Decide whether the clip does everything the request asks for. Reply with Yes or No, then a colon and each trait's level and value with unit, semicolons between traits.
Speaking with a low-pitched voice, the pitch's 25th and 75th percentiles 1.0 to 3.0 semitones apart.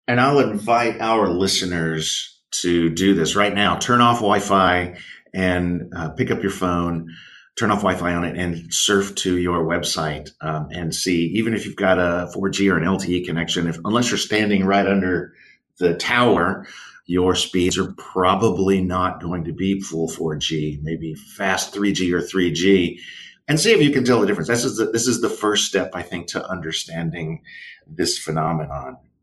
Yes: very low, 90 Hz; average, 2.7 semitones